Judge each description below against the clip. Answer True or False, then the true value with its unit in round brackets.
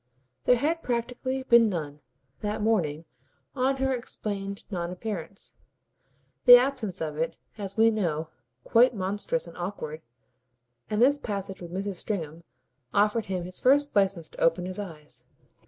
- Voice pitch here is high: True (205 Hz)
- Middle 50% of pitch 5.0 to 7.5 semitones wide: True (5.4 semitones)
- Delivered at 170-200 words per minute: False (145 wpm)